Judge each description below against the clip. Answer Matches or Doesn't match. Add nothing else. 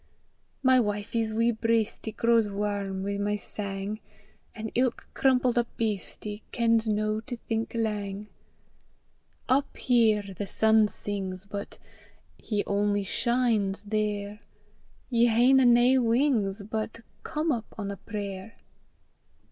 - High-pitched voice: Matches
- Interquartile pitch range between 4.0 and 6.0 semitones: Doesn't match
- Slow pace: Matches